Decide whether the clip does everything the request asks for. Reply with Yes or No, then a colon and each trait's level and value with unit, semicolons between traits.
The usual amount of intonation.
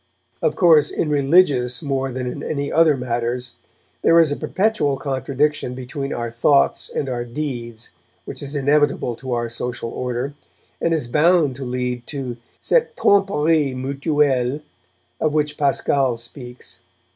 Yes: average, 3.3 semitones